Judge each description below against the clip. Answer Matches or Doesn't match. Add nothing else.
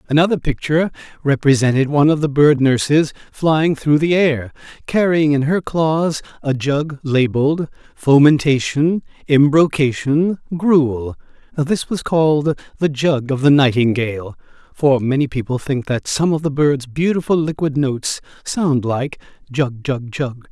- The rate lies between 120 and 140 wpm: Matches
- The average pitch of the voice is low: Doesn't match